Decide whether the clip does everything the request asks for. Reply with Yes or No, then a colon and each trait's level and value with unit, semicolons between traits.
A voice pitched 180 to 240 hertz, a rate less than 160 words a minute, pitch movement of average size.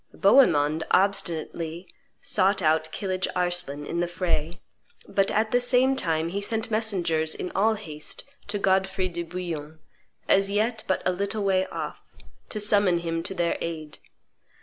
Yes: medium, 185 Hz; average, 150 wpm; average, 3.4 semitones